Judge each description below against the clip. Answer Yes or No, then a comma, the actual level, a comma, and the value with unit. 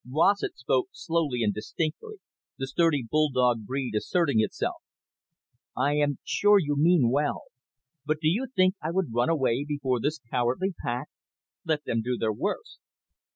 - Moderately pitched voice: Yes, medium, 145 Hz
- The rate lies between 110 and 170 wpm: Yes, average, 155 wpm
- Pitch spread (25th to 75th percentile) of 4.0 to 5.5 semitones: Yes, average, 4.7 semitones